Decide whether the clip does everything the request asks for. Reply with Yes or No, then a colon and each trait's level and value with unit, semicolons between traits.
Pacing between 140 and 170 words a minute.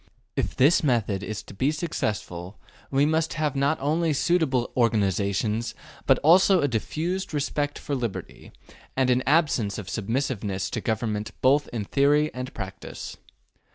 Yes: average, 145 wpm